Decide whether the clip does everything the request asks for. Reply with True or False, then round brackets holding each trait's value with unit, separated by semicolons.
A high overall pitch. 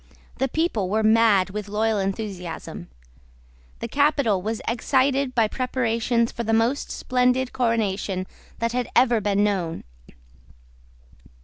True (225 Hz)